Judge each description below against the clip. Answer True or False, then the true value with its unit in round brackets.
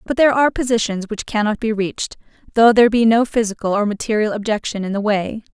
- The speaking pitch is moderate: False (220 Hz)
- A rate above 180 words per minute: True (205 wpm)